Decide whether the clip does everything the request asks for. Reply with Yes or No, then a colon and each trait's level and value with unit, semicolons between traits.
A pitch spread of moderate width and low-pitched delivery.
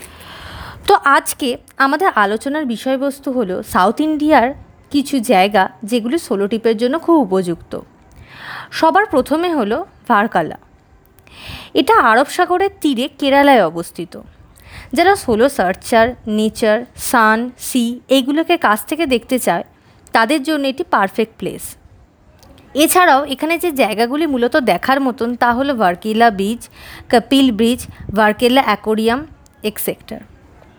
No: average, 5.0 semitones; very high, 255 Hz